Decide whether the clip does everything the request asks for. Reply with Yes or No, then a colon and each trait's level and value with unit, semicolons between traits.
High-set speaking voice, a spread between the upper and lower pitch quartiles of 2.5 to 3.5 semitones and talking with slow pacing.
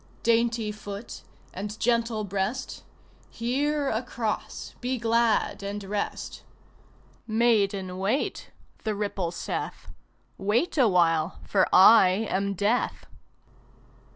Yes: high, 215 Hz; average, 3.0 semitones; slow, 95 wpm